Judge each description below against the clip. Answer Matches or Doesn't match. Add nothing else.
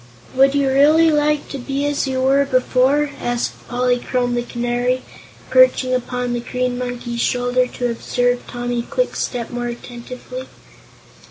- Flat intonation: Matches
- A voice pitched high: Matches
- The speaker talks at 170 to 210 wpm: Doesn't match